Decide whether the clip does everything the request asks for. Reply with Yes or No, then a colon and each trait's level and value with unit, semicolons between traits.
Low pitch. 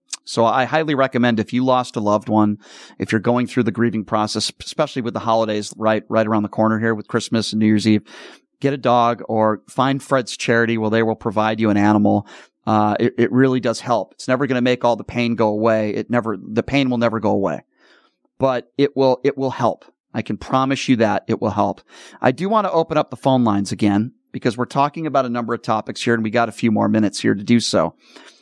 Yes: low, 115 Hz